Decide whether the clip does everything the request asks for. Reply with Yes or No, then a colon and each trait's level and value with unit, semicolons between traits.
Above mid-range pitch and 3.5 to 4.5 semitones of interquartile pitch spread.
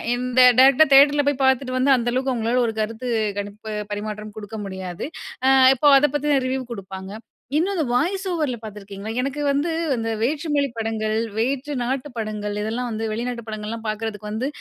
Yes: high, 235 Hz; average, 4.2 semitones